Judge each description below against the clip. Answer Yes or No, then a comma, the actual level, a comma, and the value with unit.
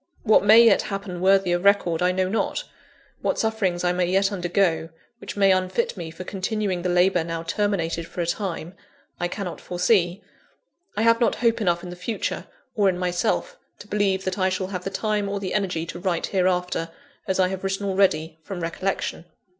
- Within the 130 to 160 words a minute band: No, average, 195 wpm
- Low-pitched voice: No, medium, 185 Hz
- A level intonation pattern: Yes, narrow, 2.3 semitones